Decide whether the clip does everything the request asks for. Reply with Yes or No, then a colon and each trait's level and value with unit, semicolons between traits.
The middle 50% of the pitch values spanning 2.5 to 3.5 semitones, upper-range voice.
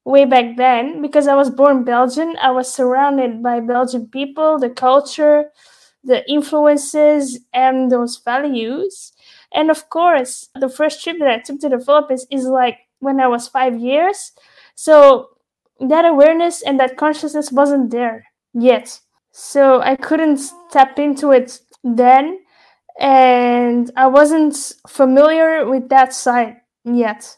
Yes: average, 2.9 semitones; very high, 270 Hz